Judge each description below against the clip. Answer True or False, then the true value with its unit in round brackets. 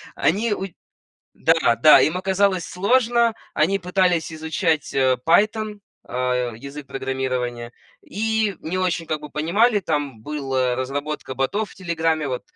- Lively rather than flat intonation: True (6.5 semitones)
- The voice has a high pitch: False (160 Hz)